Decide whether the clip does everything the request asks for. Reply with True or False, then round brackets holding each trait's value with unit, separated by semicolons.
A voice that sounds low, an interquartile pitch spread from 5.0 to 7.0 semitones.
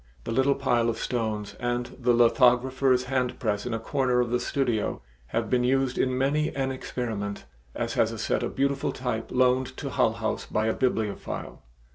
False (125 Hz; 2.4 semitones)